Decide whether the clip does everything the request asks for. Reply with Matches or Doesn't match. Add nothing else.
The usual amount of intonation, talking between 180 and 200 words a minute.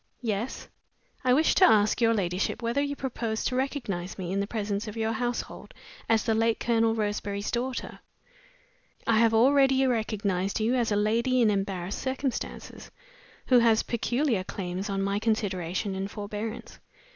Doesn't match